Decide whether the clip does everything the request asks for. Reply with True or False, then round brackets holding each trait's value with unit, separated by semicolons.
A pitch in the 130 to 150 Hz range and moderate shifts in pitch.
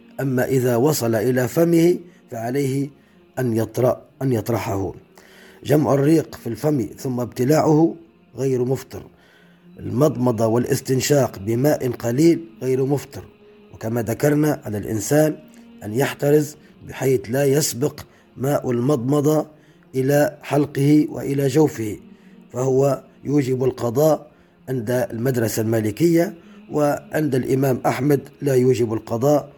True (135 Hz; 3.8 semitones)